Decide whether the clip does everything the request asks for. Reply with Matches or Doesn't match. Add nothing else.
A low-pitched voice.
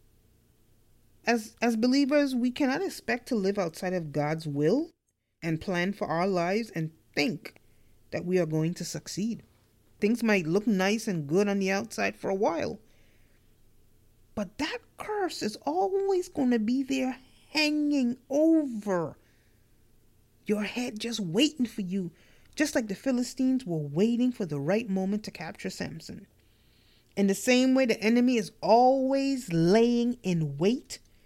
Doesn't match